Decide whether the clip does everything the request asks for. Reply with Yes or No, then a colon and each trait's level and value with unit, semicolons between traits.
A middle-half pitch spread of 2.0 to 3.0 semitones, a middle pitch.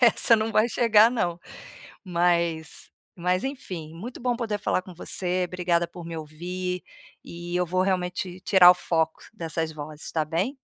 Yes: average, 2.7 semitones; medium, 180 Hz